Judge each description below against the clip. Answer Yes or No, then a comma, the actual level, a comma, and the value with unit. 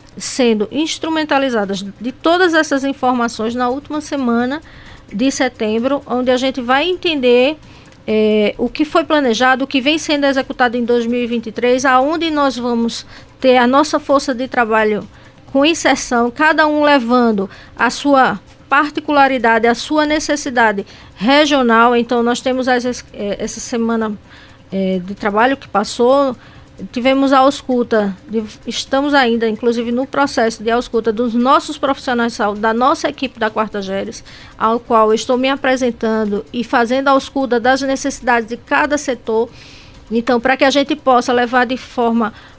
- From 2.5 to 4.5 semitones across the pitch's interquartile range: Yes, average, 3.1 semitones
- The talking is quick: No, average, 145 wpm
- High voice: Yes, very high, 250 Hz